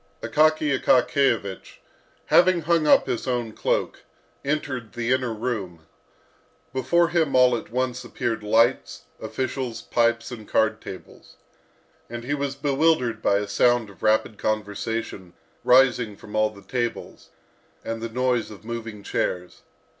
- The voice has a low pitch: Yes, low, 120 Hz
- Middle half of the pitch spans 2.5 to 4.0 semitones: Yes, average, 3.3 semitones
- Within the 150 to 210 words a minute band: No, slow, 135 wpm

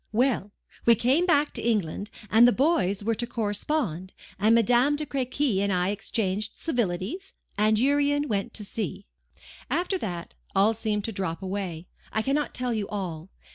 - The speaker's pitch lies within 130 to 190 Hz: No, high, 220 Hz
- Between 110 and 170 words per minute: Yes, average, 165 wpm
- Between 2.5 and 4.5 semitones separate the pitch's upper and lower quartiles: No, average, 5.2 semitones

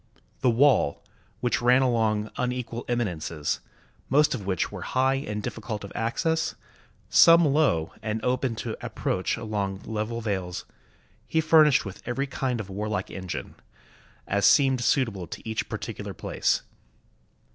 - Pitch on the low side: Yes, low, 115 Hz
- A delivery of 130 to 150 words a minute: Yes, average, 140 wpm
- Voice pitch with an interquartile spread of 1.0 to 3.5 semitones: No, average, 4.4 semitones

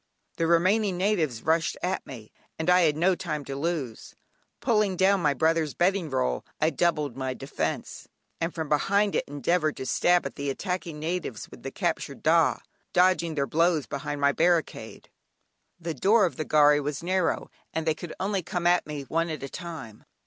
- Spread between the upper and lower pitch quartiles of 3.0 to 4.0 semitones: Yes, average, 3.6 semitones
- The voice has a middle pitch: Yes, medium, 165 Hz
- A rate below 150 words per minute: No, average, 185 wpm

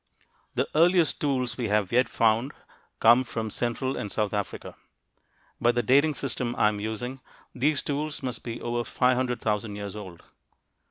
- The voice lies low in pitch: Yes, low, 120 Hz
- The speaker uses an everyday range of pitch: Yes, average, 3.4 semitones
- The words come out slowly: No, average, 150 wpm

